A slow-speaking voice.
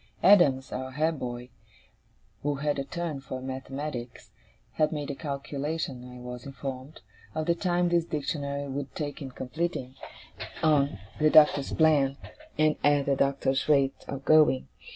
No: average, 150 wpm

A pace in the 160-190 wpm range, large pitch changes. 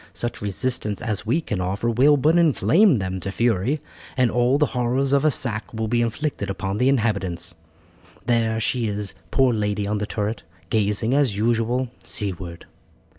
No: average, 170 wpm; average, 3.9 semitones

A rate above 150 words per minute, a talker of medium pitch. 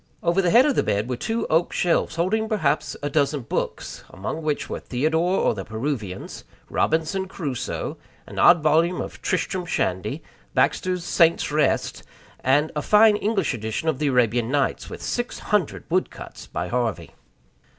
Yes: average, 165 wpm; medium, 160 Hz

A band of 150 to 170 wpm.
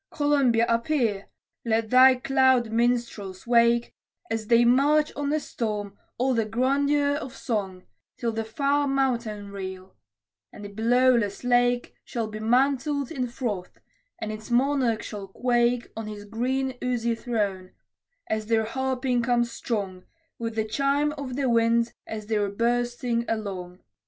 No: average, 140 wpm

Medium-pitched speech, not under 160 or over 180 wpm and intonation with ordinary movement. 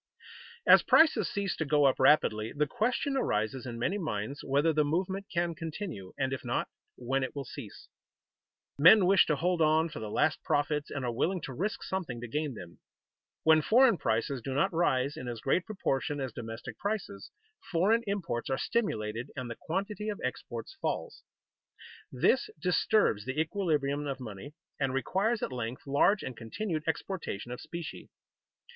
No: medium, 150 Hz; average, 175 wpm; wide, 6.8 semitones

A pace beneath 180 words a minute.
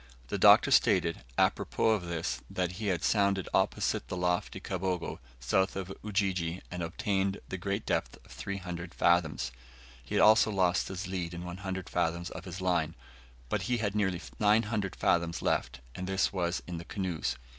Yes: average, 165 wpm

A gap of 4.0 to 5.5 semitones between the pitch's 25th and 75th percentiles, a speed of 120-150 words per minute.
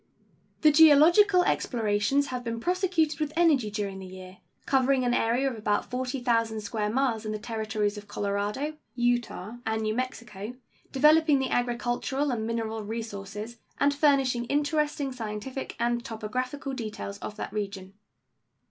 Yes: average, 4.4 semitones; average, 140 wpm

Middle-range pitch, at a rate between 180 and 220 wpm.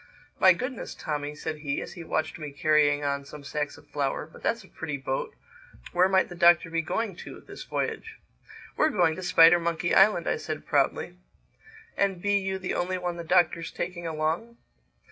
Yes: medium, 170 Hz; average, 185 wpm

